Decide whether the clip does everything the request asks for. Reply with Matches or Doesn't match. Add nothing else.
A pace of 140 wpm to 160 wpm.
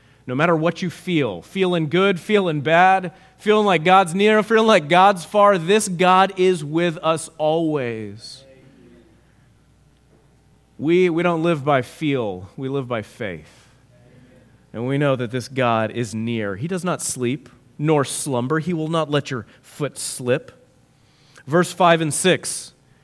Matches